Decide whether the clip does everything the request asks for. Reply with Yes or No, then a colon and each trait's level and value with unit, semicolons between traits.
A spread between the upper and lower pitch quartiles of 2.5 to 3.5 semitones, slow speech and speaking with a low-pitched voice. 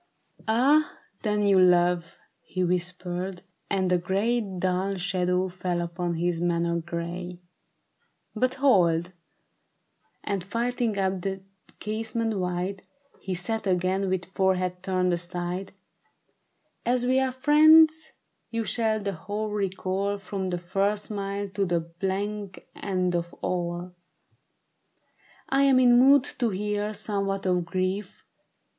No: average, 2.8 semitones; slow, 130 wpm; high, 190 Hz